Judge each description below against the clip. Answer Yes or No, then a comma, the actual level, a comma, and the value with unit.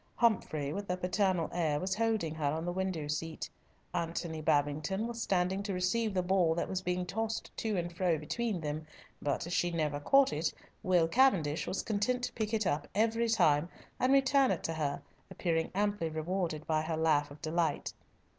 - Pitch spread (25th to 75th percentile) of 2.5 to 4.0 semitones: No, average, 4.5 semitones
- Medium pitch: Yes, medium, 175 Hz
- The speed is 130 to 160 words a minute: No, average, 190 wpm